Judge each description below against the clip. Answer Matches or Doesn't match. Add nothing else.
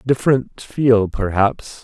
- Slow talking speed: Matches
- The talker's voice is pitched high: Doesn't match